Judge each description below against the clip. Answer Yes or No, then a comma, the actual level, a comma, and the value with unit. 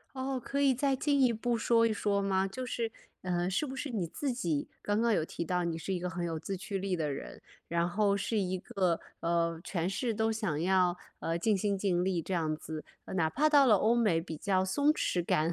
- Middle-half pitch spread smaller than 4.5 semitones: No, average, 5.0 semitones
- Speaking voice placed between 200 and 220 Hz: No, high, 190 Hz